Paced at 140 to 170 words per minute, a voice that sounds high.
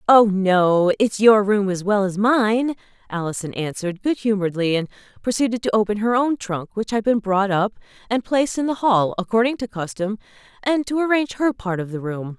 No: average, 200 wpm; high, 215 Hz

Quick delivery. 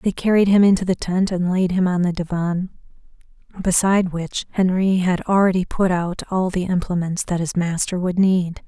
No: average, 185 wpm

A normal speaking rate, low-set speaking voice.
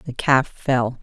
Yes: average, 175 wpm; low, 125 Hz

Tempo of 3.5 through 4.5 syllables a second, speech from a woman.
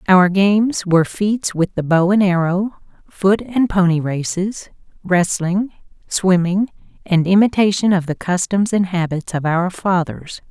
Yes: 4.2 syllables/s; female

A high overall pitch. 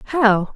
Yes: high, 235 Hz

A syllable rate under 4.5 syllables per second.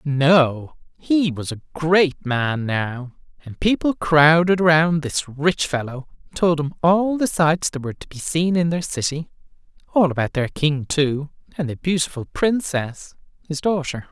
Yes: 4.2 syllables/s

